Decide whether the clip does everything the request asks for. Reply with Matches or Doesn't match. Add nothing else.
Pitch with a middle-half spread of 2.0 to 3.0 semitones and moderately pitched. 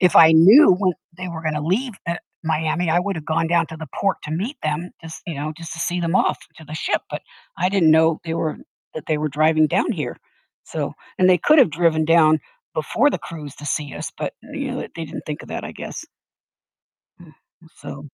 Matches